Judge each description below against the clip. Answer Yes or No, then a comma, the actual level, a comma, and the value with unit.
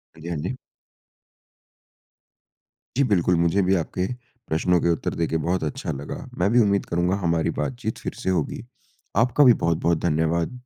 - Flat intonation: No, average, 3.3 semitones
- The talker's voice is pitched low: Yes, very low, 85 Hz